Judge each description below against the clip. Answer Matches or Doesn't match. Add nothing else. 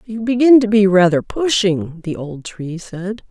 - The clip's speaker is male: Doesn't match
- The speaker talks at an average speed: Matches